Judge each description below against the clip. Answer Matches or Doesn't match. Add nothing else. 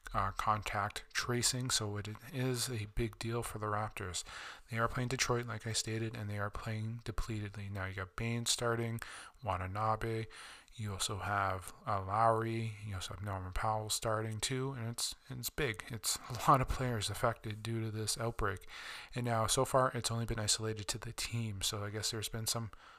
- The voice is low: Matches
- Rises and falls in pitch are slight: Matches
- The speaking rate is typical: Matches